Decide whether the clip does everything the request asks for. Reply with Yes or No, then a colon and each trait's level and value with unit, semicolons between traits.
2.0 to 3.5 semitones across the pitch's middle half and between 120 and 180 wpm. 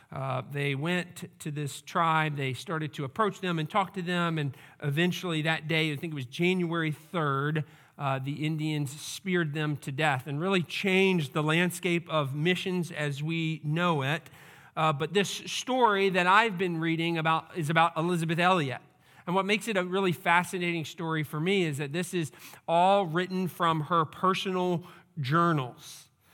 Yes: average, 3.0 semitones; average, 175 wpm